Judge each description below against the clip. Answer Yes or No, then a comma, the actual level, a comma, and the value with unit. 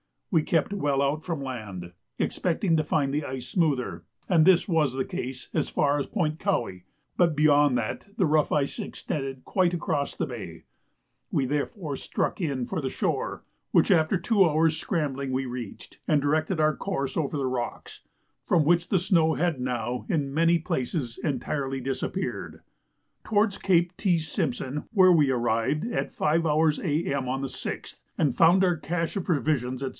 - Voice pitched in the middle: Yes, medium, 150 Hz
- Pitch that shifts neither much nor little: Yes, average, 4.0 semitones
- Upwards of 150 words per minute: Yes, average, 170 wpm